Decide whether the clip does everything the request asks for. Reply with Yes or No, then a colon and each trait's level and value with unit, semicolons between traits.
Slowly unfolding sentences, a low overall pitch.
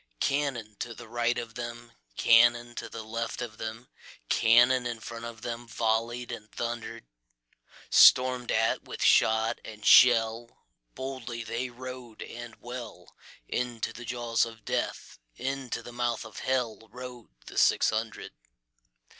Yes: slow, 110 wpm; low, 115 Hz